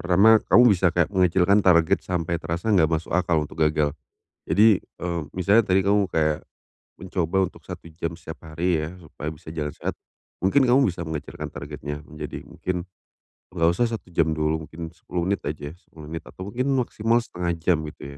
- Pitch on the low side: Yes, very low, 85 Hz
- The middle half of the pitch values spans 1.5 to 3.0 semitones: No, average, 3.4 semitones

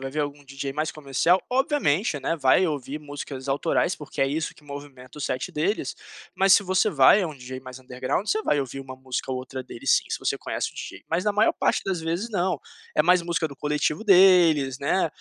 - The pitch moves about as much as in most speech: Yes, average, 4.9 semitones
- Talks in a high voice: No, medium, 150 Hz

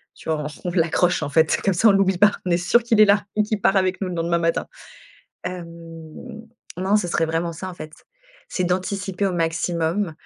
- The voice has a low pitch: No, medium, 180 Hz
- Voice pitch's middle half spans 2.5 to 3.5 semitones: Yes, average, 2.8 semitones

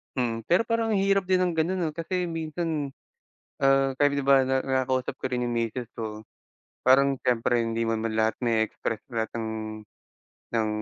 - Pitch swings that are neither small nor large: No, wide, 6.2 semitones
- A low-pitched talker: Yes, low, 130 Hz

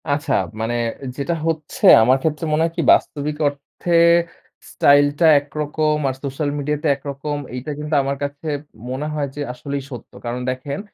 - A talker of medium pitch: Yes, medium, 145 Hz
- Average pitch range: No, narrow, 1.7 semitones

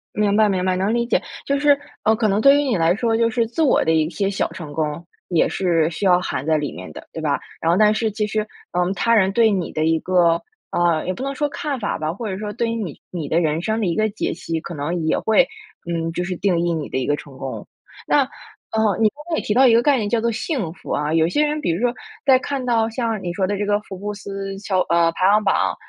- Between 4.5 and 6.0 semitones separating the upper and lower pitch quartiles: Yes, average, 5.2 semitones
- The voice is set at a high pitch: Yes, high, 200 Hz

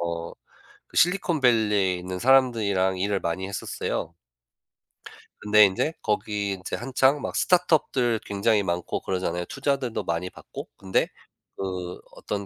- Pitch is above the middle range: No, low, 100 Hz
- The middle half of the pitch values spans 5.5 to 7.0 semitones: No, average, 5.1 semitones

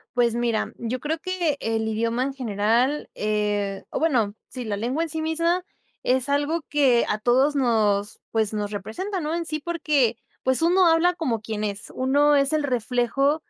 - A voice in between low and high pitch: No, very high, 255 Hz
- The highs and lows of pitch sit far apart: Yes, wide, 5.7 semitones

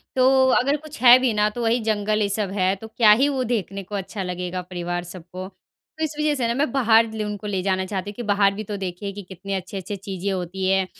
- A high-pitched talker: Yes, high, 205 Hz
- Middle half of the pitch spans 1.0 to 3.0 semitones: No, average, 3.6 semitones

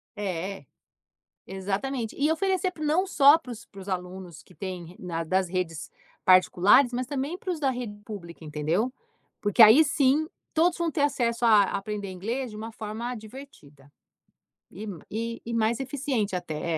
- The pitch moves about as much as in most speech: No, wide, 6.5 semitones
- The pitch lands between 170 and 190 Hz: No, high, 220 Hz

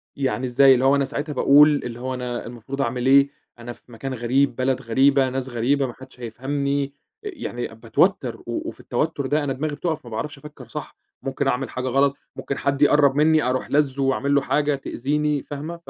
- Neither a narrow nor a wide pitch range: No, narrow, 2.2 semitones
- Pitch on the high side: No, low, 135 Hz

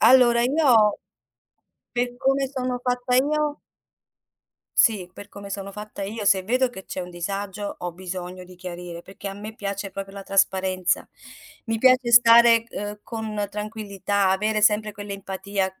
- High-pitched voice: Yes, high, 205 Hz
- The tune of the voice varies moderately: Yes, average, 3.6 semitones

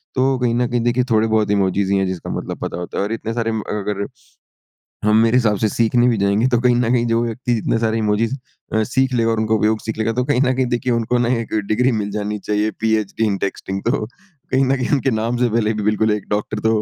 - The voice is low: Yes, low, 115 Hz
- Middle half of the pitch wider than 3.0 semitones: No, narrow, 2.4 semitones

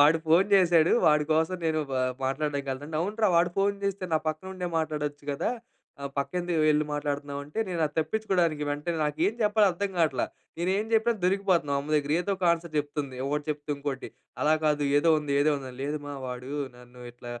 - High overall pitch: No, medium, 155 Hz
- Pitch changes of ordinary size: Yes, average, 3.8 semitones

